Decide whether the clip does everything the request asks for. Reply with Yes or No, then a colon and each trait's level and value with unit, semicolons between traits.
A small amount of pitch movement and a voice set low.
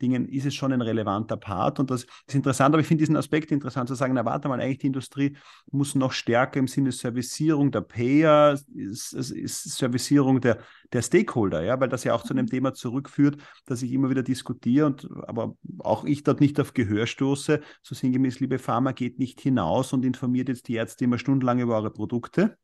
Yes: narrow, 2.3 semitones; low, 130 Hz